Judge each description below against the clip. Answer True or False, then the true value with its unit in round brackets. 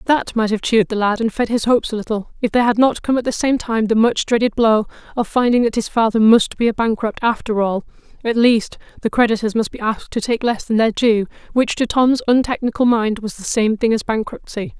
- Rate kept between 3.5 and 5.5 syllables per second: False (5.8 syllables/s)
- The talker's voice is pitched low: False (225 Hz)